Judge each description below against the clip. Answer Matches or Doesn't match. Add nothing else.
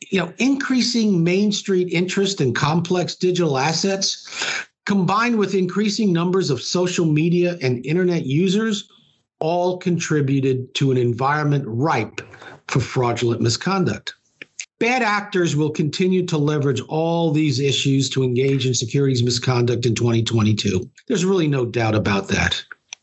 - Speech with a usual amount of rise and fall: Doesn't match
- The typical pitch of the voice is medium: Matches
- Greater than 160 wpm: Doesn't match